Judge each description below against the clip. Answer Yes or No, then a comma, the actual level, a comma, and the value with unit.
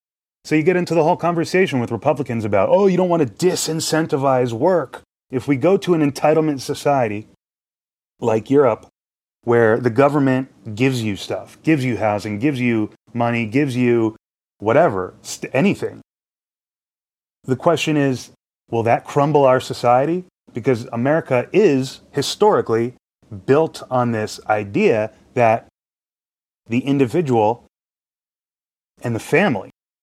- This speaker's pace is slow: Yes, slow, 130 wpm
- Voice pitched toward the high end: No, low, 130 Hz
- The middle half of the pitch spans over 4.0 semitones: Yes, average, 4.6 semitones